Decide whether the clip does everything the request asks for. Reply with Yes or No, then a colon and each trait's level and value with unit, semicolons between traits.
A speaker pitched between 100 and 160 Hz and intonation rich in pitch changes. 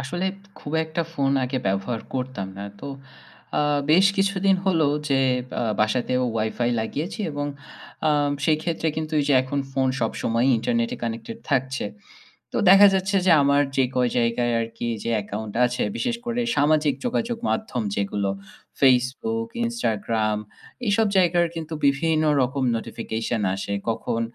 Yes: low, 135 Hz; wide, 6.7 semitones